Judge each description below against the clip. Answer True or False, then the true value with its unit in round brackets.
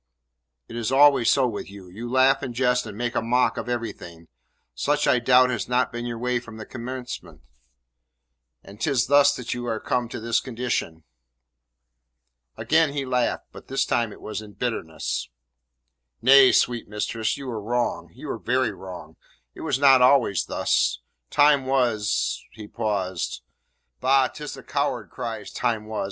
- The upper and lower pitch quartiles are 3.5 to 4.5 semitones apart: False (3.1 semitones)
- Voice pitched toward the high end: False (120 Hz)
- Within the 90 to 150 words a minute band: False (170 wpm)